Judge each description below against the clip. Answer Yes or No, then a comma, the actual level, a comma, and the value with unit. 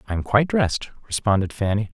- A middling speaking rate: Yes, average, 180 wpm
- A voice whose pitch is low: Yes, low, 110 Hz